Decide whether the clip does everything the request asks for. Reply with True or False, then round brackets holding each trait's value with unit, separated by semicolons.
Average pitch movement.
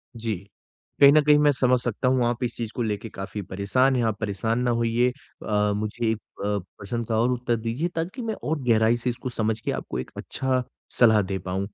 True (3.0 semitones)